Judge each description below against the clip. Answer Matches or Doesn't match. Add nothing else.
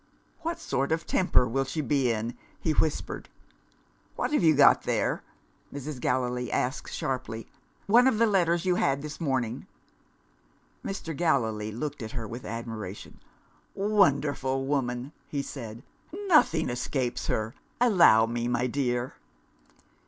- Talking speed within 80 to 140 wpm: Matches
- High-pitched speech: Doesn't match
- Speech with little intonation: Doesn't match